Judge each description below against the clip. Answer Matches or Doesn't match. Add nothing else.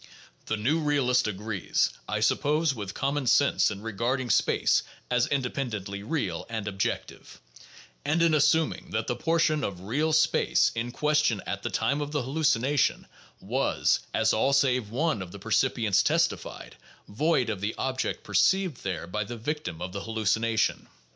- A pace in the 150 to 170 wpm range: Matches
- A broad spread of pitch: Matches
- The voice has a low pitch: Matches